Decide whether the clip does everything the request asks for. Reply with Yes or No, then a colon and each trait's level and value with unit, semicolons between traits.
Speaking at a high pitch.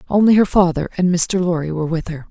No: medium, 175 Hz